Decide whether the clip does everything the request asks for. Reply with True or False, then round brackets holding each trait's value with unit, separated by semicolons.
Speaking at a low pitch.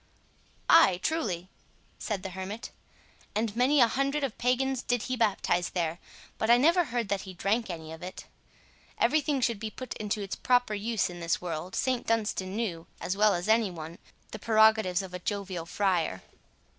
False (210 Hz)